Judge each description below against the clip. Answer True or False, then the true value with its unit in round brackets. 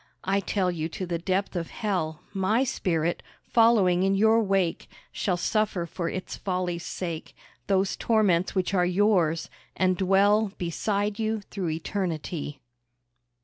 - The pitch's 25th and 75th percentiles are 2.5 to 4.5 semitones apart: True (2.9 semitones)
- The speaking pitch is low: False (185 Hz)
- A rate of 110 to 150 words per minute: True (140 wpm)